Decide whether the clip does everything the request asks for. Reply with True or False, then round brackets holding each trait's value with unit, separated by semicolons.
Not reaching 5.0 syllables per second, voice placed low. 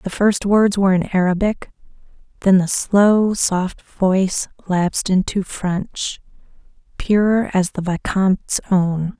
False (3.7 syllables/s; 190 Hz)